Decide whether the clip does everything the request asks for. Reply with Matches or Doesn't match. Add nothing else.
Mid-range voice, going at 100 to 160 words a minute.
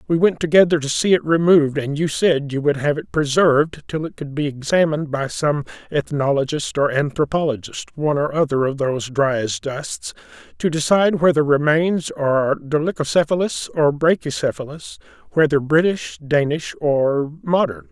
Matches